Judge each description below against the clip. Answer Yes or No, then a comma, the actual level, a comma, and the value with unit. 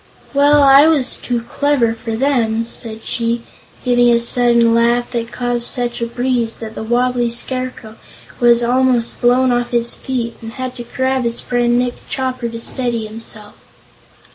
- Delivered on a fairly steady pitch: Yes, narrow, 1.6 semitones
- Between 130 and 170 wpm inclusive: Yes, average, 165 wpm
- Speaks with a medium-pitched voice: No, high, 240 Hz